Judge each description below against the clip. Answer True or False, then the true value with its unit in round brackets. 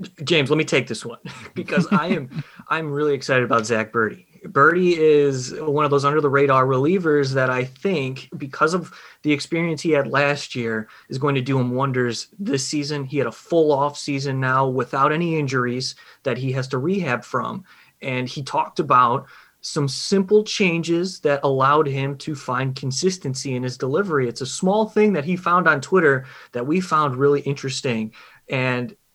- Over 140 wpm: True (185 wpm)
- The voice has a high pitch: False (140 Hz)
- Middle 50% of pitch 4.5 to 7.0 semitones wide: False (3.4 semitones)